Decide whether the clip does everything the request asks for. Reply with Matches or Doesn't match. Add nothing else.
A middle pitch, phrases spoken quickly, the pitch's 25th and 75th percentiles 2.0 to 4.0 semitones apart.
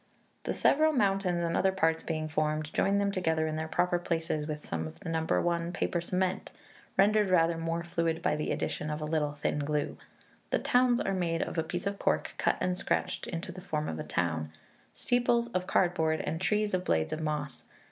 Matches